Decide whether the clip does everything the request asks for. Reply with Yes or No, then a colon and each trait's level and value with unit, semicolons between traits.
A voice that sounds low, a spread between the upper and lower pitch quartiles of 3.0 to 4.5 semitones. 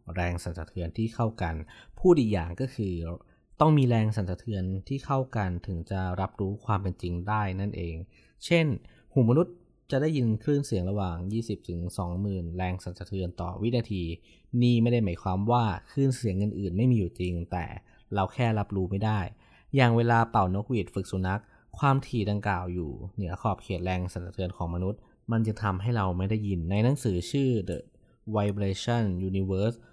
Yes: low, 100 Hz; average, 4.0 semitones